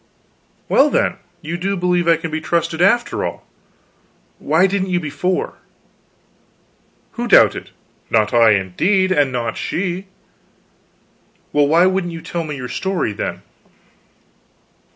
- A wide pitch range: No, average, 4.3 semitones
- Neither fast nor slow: No, slow, 130 wpm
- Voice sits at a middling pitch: Yes, medium, 170 Hz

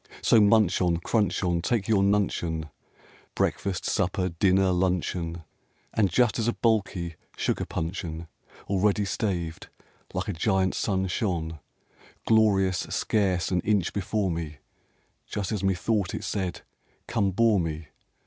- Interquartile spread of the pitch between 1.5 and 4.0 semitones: Yes, average, 3.1 semitones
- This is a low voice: Yes, very low, 95 Hz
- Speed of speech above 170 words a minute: No, average, 140 wpm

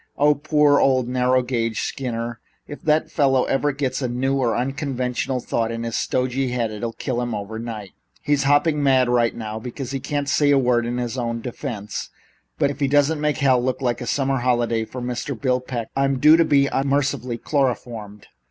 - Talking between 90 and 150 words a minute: No, average, 195 wpm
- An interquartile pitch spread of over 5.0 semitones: No, average, 2.8 semitones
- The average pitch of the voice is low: Yes, low, 125 Hz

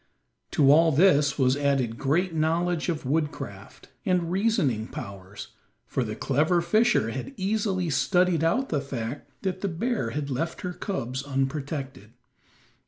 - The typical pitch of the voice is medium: Yes, medium, 155 Hz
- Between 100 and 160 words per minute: Yes, average, 140 wpm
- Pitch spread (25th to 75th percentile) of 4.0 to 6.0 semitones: Yes, average, 5.2 semitones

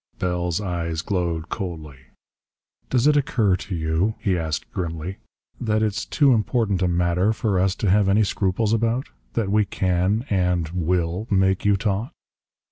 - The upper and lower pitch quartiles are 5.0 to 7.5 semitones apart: No, average, 3.6 semitones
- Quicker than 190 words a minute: No, average, 155 wpm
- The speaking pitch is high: No, very low, 95 Hz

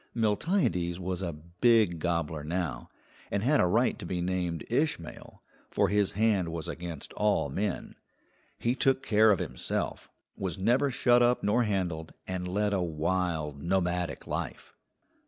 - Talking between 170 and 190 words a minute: No, average, 150 wpm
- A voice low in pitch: Yes, very low, 90 Hz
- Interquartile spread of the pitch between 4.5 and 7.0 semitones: No, average, 4.0 semitones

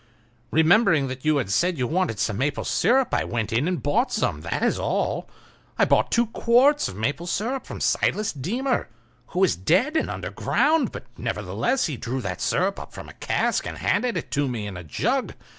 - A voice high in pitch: No, medium, 170 Hz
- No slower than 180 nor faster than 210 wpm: Yes, average, 185 wpm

